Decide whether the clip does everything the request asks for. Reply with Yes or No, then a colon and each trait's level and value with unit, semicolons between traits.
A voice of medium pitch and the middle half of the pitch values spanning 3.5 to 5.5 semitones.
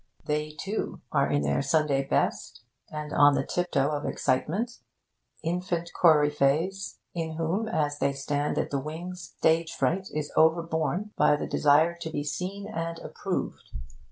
No: medium, 160 Hz; average, 2.9 semitones